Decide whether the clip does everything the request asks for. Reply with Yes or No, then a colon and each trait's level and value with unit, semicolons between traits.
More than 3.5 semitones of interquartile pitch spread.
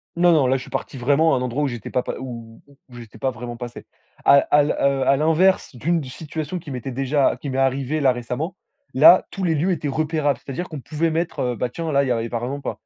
Yes: average, 3.9 semitones